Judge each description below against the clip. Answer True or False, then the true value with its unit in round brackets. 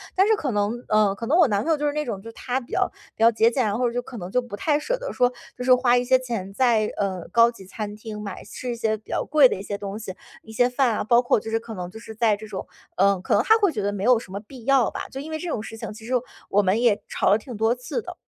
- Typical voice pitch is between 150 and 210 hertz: False (230 Hz)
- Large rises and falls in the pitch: False (3.5 semitones)